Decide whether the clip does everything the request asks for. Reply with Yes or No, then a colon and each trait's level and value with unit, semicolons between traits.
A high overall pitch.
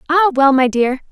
Yes: very high, 285 Hz